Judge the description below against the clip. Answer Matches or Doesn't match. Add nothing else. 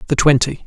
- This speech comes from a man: Matches